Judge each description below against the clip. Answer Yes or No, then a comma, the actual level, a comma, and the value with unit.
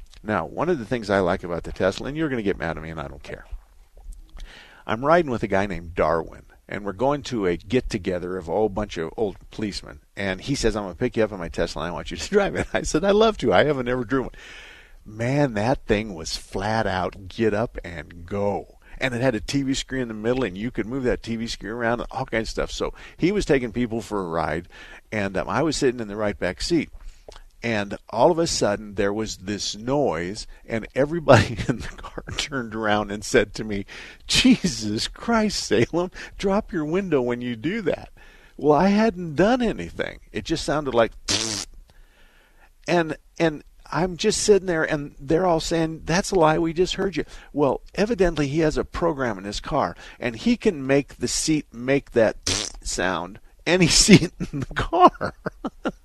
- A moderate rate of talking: No, fast, 220 wpm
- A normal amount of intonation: No, wide, 7.4 semitones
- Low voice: Yes, low, 120 Hz